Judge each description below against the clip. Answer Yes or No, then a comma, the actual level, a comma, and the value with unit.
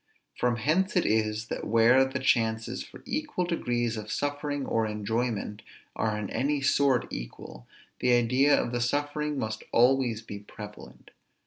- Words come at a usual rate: Yes, average, 150 wpm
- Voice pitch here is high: No, low, 120 Hz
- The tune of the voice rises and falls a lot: No, average, 4.4 semitones